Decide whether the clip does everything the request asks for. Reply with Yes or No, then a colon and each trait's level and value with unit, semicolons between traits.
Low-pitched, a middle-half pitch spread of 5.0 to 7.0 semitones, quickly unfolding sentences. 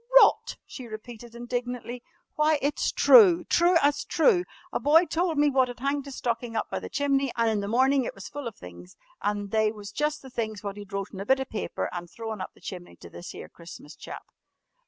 No: high, 240 Hz; wide, 5.5 semitones; fast, 225 wpm